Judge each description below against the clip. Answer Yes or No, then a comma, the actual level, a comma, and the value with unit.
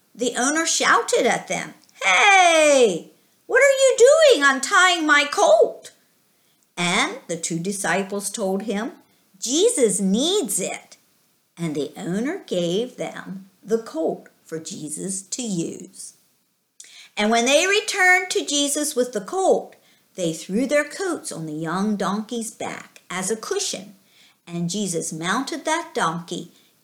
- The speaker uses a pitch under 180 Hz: No, high, 235 Hz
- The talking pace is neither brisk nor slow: No, slow, 130 wpm